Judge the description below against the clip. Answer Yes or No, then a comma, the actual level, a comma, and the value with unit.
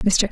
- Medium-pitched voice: No, high, 200 Hz